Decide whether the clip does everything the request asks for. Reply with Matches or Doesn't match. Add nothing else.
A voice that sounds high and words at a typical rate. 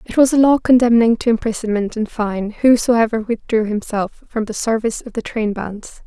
Matches